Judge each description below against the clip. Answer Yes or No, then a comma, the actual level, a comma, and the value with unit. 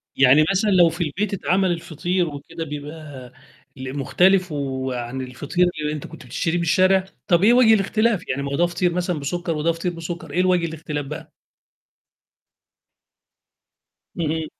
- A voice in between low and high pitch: Yes, medium, 165 Hz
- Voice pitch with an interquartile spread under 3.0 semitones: No, average, 3.9 semitones